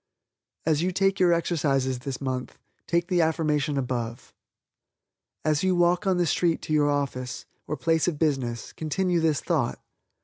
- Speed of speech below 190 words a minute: Yes, average, 160 wpm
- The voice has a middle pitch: Yes, medium, 155 Hz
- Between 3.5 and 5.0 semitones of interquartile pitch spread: Yes, average, 4.1 semitones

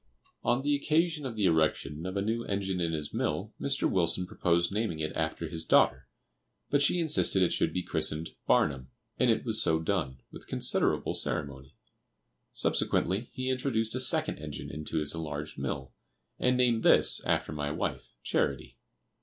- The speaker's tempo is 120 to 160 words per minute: No, average, 170 wpm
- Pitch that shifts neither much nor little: No, wide, 7.2 semitones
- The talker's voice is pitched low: Yes, very low, 85 Hz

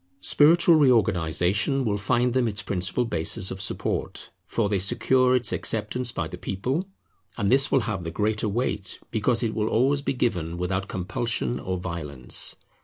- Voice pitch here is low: Yes, low, 105 Hz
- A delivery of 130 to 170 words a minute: Yes, average, 165 wpm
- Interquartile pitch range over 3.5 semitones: Yes, average, 5.3 semitones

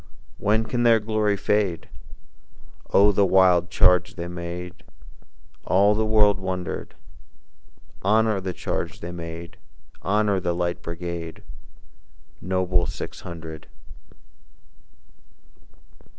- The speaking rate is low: Yes, slow, 100 wpm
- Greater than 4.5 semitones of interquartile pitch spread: No, average, 3.1 semitones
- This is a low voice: Yes, very low, 95 Hz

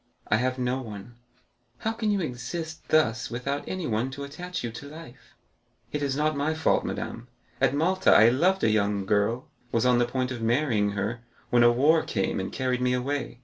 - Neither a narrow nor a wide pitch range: Yes, average, 4.3 semitones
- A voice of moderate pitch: No, low, 125 Hz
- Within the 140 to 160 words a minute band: No, average, 190 wpm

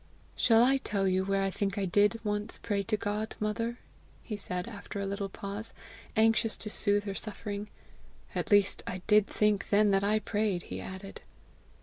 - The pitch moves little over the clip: Yes, narrow, 1.4 semitones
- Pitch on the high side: Yes, high, 205 Hz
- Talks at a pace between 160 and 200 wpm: Yes, average, 185 wpm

